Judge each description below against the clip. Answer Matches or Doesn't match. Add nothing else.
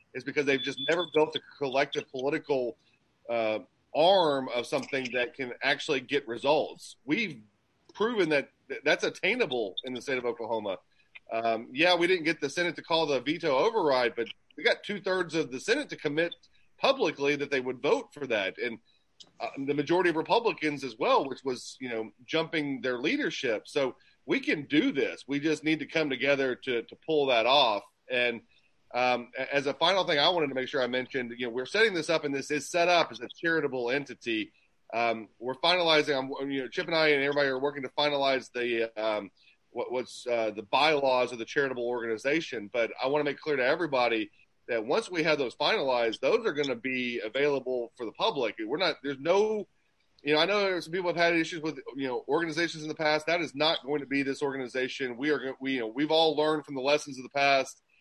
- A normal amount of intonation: Matches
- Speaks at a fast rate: Matches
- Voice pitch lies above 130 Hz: Matches